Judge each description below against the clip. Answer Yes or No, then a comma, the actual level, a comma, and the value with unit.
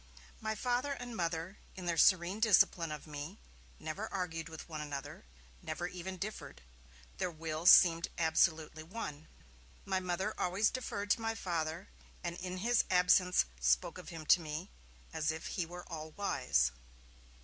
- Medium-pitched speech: Yes, medium, 175 Hz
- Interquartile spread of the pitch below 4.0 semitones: Yes, average, 3.2 semitones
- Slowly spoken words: No, average, 155 wpm